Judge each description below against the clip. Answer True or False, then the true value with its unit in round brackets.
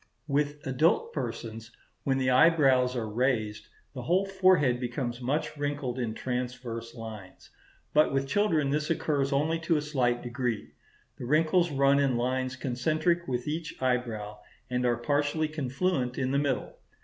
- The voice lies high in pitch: False (135 Hz)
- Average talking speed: True (150 wpm)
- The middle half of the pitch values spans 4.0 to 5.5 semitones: False (3.6 semitones)